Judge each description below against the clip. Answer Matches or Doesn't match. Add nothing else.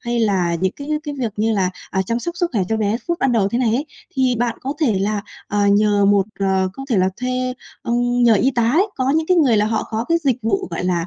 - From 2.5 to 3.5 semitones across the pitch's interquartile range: Doesn't match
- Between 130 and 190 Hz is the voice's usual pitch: Doesn't match